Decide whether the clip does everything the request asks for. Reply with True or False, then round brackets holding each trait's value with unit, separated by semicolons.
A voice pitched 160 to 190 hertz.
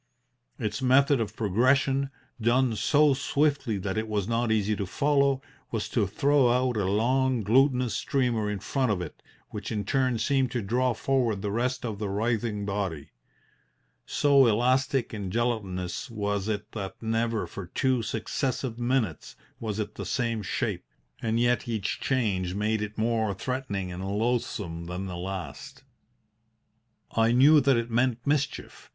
False (115 Hz)